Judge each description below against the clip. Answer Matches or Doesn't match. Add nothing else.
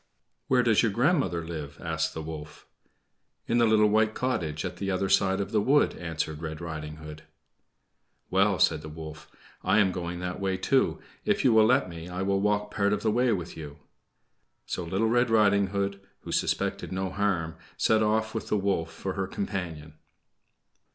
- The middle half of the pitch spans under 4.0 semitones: Doesn't match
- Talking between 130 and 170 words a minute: Doesn't match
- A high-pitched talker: Doesn't match